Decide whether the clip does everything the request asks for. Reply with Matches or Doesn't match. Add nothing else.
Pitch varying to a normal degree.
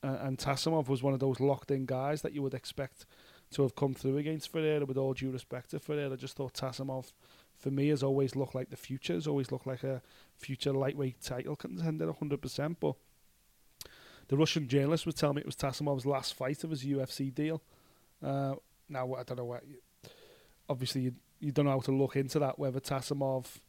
Doesn't match